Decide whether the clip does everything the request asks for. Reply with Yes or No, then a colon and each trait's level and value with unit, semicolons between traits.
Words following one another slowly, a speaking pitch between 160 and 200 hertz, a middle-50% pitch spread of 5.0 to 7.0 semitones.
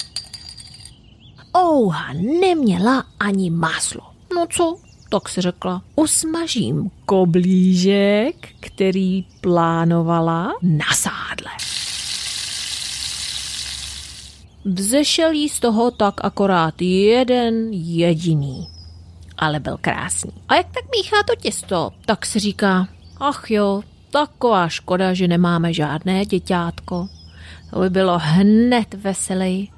Yes: slow, 95 wpm; high, 190 Hz; wide, 5.4 semitones